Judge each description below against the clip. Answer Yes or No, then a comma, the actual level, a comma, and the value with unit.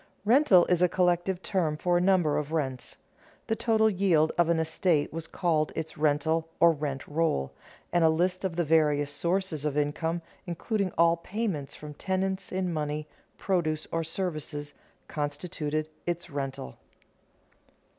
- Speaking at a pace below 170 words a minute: Yes, average, 150 wpm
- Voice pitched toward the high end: No, medium, 165 Hz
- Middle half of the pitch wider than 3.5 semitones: No, average, 3.2 semitones